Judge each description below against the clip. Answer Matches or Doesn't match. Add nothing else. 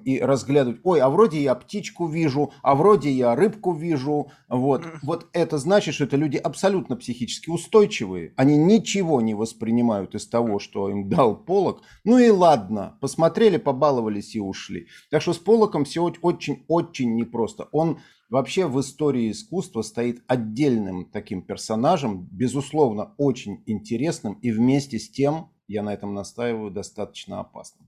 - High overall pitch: Doesn't match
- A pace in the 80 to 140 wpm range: Doesn't match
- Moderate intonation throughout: Doesn't match